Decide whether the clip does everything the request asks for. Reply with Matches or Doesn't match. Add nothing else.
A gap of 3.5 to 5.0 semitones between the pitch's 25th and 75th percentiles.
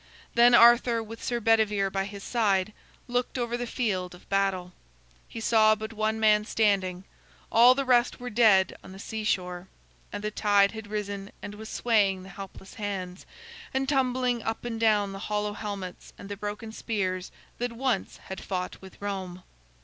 Doesn't match